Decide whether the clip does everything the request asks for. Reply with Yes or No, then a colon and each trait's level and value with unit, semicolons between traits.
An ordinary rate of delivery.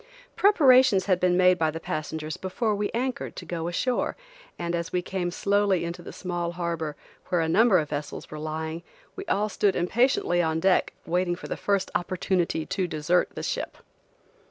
Yes: average, 180 wpm